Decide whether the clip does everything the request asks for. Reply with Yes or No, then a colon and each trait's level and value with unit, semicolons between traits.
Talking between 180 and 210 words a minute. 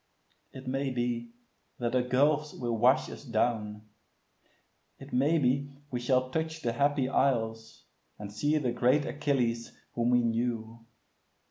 No: average, 140 wpm